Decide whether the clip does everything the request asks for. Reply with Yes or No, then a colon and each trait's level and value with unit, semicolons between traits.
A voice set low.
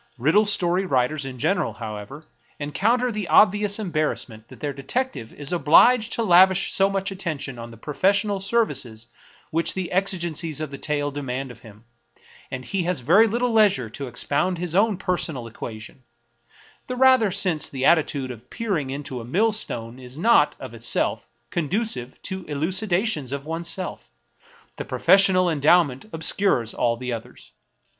No: medium, 165 Hz